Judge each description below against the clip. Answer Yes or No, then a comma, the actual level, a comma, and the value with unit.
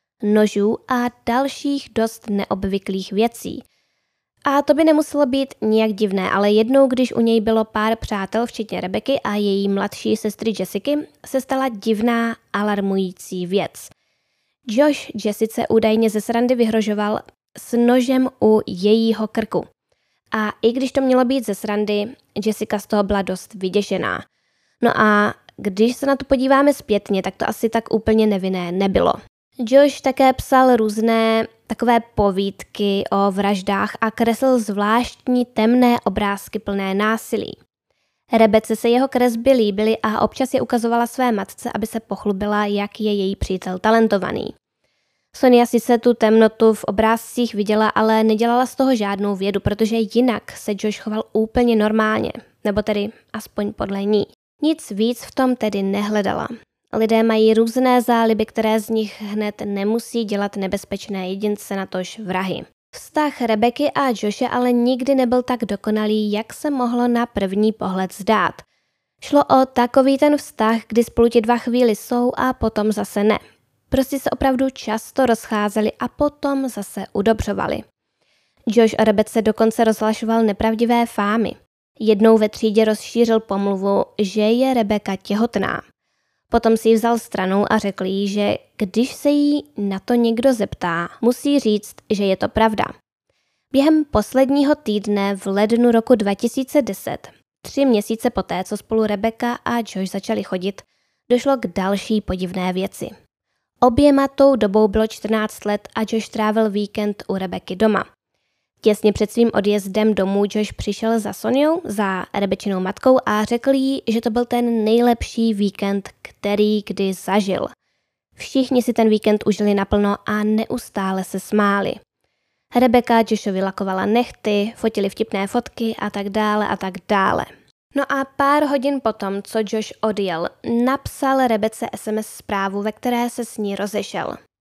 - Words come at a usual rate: Yes, average, 150 wpm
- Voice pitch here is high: Yes, high, 220 Hz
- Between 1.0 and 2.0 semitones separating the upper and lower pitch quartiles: No, average, 2.7 semitones